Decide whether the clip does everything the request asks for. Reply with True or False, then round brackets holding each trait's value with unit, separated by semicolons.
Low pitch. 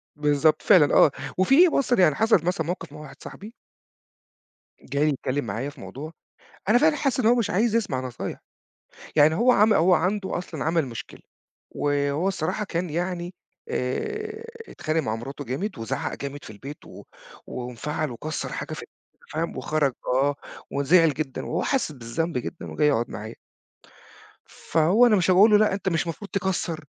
False (160 Hz)